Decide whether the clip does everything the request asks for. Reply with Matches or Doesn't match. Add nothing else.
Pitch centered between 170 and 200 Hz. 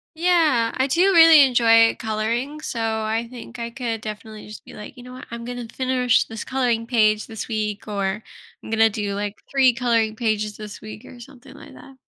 Doesn't match